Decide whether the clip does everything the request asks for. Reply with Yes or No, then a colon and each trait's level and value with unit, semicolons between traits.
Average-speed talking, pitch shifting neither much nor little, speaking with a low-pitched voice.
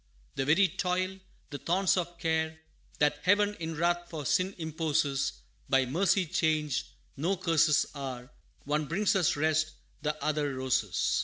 No: average, 145 wpm; average, 3.4 semitones; medium, 160 Hz